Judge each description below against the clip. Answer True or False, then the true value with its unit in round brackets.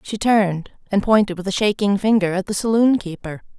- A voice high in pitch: True (200 Hz)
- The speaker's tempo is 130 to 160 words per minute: False (200 wpm)